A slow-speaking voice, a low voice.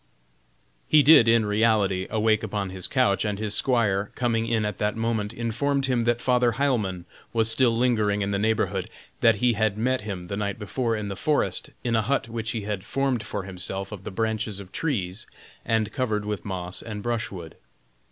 No: average, 190 wpm; low, 110 Hz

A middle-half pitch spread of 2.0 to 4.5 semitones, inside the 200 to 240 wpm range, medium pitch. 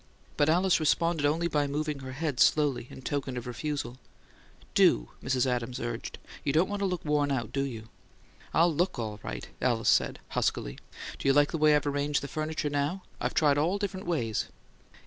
Yes: average, 3.6 semitones; fast, 205 wpm; medium, 145 Hz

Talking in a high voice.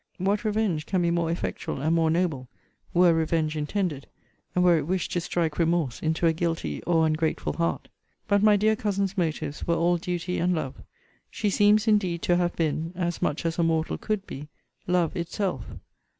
No: medium, 170 Hz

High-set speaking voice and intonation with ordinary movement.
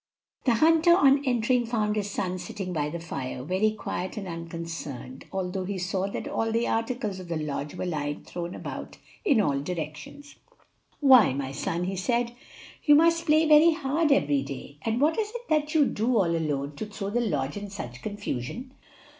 No: high, 200 Hz; wide, 7.6 semitones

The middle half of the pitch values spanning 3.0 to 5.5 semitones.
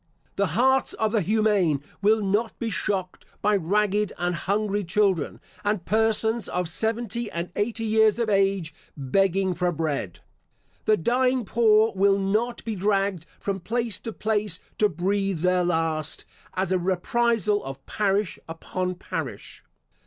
Yes: average, 3.3 semitones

